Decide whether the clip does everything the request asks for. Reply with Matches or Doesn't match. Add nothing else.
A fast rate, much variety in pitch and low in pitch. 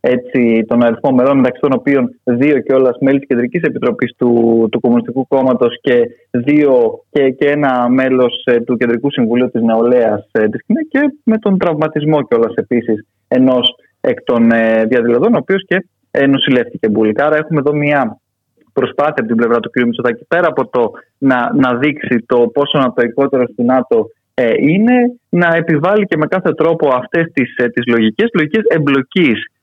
Doesn't match